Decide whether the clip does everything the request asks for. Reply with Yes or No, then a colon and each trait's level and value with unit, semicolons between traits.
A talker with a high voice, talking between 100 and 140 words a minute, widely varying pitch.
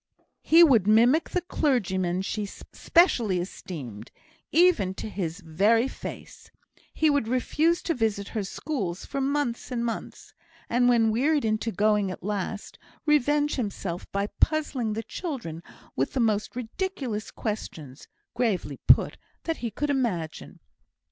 Yes: high, 225 Hz; slow, 135 wpm; wide, 6.3 semitones